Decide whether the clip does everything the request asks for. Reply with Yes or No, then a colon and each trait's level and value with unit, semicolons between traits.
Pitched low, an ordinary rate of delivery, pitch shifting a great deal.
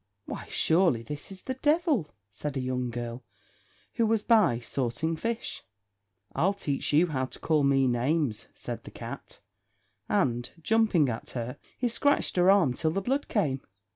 No: medium, 155 Hz; average, 165 wpm; wide, 8.4 semitones